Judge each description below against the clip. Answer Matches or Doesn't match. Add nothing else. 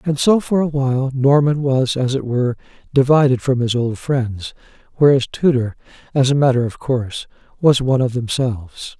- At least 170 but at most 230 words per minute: Matches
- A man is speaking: Matches